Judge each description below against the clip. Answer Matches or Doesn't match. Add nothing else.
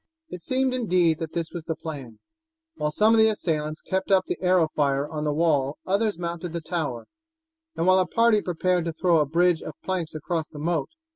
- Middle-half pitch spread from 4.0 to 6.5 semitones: Doesn't match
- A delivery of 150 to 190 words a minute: Doesn't match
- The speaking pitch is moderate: Matches